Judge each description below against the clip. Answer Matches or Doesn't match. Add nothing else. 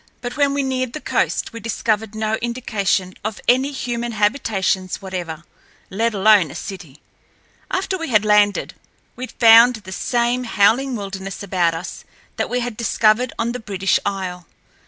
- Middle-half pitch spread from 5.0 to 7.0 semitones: Doesn't match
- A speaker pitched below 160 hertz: Doesn't match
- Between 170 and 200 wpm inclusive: Doesn't match